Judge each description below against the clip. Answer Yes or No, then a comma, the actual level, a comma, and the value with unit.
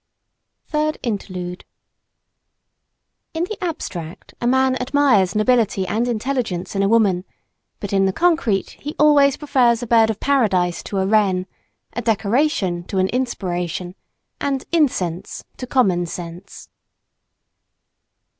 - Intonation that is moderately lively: No, wide, 6.0 semitones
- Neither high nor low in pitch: No, high, 220 Hz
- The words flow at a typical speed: No, slow, 125 wpm